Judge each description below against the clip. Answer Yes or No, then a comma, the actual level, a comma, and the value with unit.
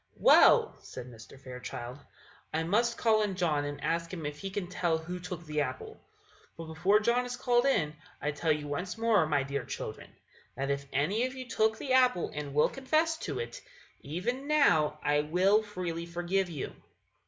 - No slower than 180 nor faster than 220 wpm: Yes, average, 185 wpm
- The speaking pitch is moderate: Yes, medium, 175 Hz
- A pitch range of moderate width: No, wide, 6.9 semitones